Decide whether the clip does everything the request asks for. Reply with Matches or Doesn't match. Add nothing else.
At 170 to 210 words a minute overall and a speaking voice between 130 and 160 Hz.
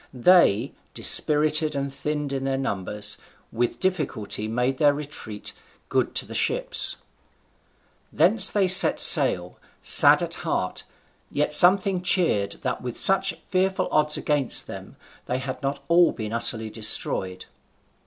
Doesn't match